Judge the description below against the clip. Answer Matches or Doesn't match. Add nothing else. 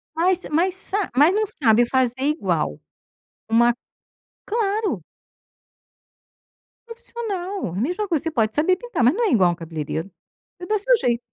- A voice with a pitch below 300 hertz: Doesn't match